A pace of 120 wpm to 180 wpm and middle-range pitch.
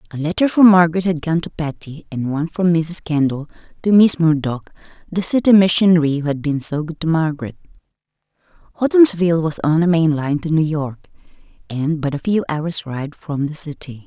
No: average, 190 wpm; medium, 160 Hz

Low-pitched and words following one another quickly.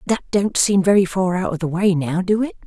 No: high, 190 Hz; fast, 270 wpm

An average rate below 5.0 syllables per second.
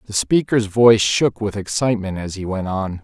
No: 5.2 syllables/s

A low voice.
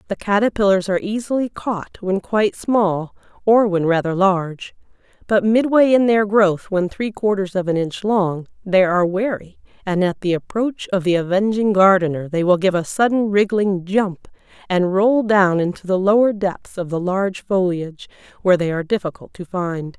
No: high, 195 Hz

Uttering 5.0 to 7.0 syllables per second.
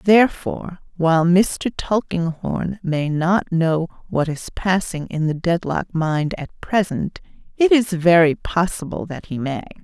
No: 4.0 syllables/s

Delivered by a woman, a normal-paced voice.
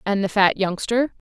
Yes: female; average, 180 wpm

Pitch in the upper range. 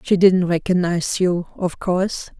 No: medium, 180 Hz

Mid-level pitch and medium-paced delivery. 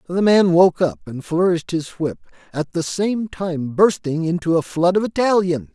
Yes: medium, 175 Hz; average, 190 wpm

